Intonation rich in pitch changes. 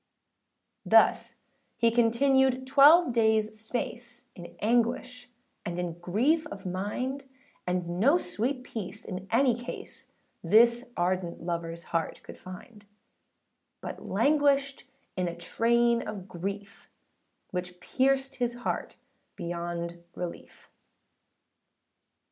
Yes: wide, 5.9 semitones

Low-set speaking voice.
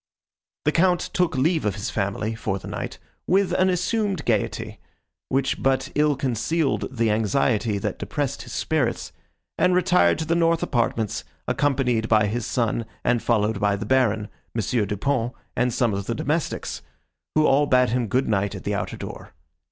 Yes: low, 125 Hz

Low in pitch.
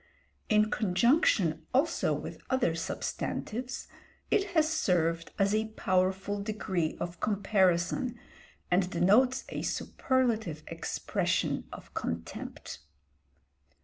No: high, 200 Hz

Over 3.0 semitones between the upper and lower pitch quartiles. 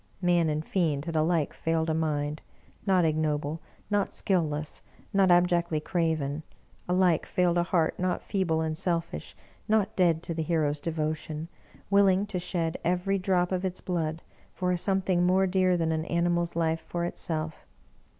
No: narrow, 2.4 semitones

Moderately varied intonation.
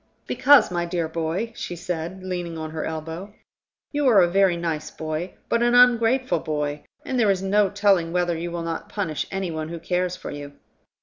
Yes: average, 3.6 semitones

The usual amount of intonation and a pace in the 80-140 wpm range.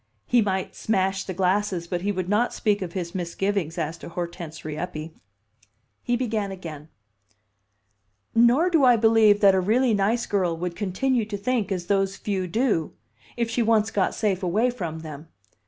No: average, 4.1 semitones; average, 170 wpm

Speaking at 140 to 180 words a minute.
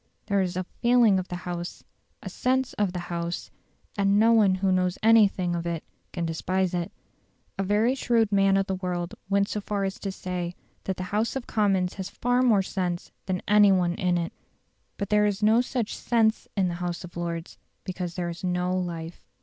No: average, 200 wpm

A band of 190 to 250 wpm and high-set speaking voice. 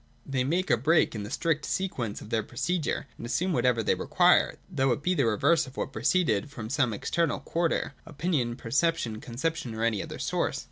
No: average, 200 wpm; low, 135 Hz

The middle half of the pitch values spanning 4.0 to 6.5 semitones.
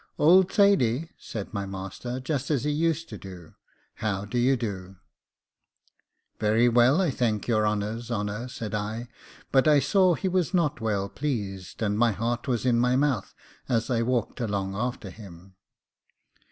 Yes: average, 4.6 semitones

